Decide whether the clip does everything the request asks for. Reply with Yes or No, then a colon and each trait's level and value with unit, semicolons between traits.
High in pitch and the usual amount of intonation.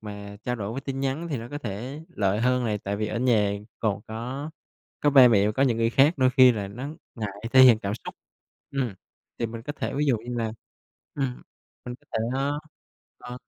No: low, 120 Hz; average, 3.9 semitones